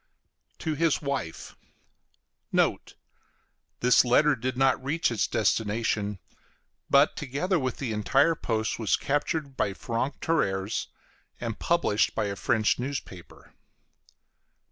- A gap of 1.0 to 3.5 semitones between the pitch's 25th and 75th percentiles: No, average, 4.9 semitones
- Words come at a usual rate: No, slow, 120 wpm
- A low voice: Yes, low, 125 Hz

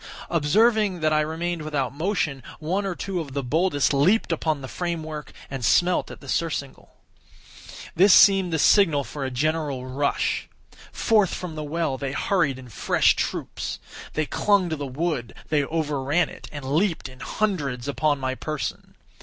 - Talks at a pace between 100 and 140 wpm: No, average, 165 wpm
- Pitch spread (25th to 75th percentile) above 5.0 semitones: No, average, 4.0 semitones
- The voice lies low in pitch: No, medium, 155 Hz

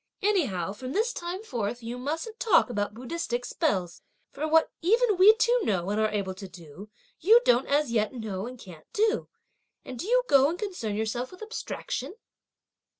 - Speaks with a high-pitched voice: Yes, very high, 255 Hz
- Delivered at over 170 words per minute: Yes, average, 180 wpm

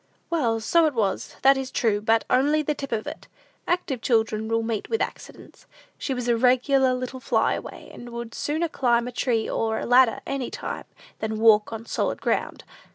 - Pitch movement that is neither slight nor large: Yes, average, 3.2 semitones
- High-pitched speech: Yes, high, 245 Hz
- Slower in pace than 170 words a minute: No, average, 195 wpm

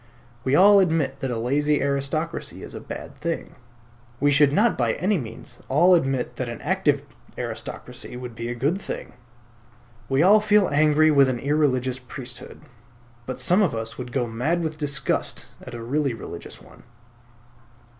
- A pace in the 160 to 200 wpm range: Yes, average, 165 wpm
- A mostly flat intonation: No, average, 4.2 semitones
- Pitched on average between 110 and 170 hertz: Yes, medium, 140 Hz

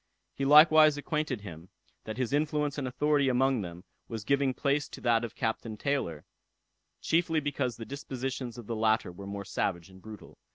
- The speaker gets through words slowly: No, average, 175 wpm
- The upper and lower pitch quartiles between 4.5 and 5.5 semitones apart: Yes, average, 4.8 semitones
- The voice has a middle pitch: No, low, 125 Hz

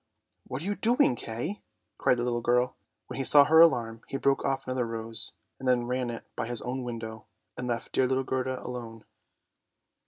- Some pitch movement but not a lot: No, narrow, 2.2 semitones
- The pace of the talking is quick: Yes, fast, 210 wpm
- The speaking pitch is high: No, low, 125 Hz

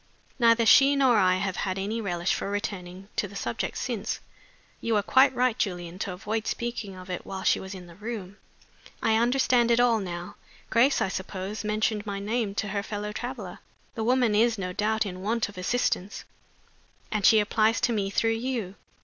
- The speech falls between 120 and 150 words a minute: No, average, 190 wpm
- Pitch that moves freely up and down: No, average, 3.2 semitones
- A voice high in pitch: Yes, high, 210 Hz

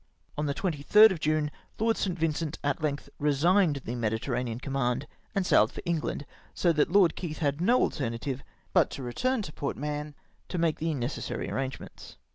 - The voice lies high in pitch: No, medium, 150 Hz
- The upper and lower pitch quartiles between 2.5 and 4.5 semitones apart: Yes, average, 3.9 semitones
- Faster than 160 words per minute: Yes, average, 180 wpm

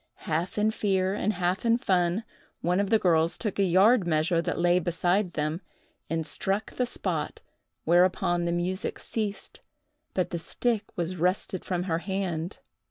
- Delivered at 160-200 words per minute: Yes, average, 165 wpm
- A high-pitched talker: No, medium, 180 Hz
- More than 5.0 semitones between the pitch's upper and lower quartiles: No, narrow, 2.6 semitones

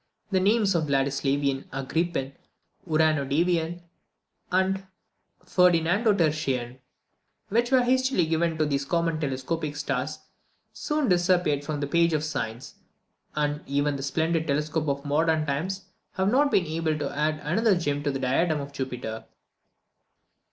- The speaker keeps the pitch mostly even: No, average, 3.8 semitones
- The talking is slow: Yes, slow, 130 wpm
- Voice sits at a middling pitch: Yes, medium, 155 Hz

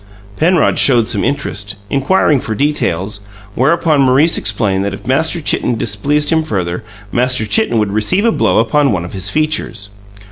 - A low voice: Yes, low, 125 Hz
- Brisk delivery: No, average, 165 wpm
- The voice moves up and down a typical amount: No, wide, 6.6 semitones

